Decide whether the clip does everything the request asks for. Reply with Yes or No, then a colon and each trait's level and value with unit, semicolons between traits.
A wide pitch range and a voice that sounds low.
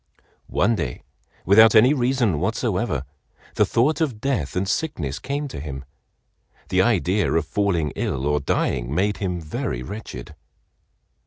Yes: wide, 7.9 semitones; very low, 95 Hz